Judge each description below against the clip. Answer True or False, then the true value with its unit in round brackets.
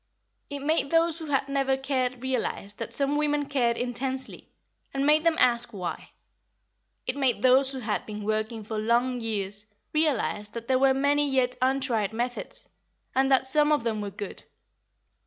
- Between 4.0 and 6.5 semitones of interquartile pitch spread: False (3.3 semitones)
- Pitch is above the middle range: True (260 Hz)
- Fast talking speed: False (170 wpm)